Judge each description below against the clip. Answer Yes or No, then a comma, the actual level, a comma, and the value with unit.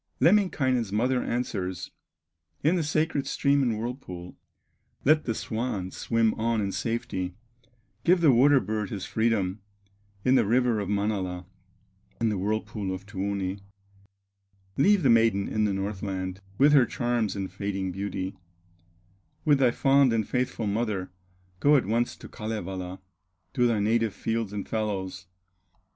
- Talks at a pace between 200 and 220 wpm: No, average, 140 wpm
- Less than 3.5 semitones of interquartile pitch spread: No, average, 4.2 semitones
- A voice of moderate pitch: No, low, 110 Hz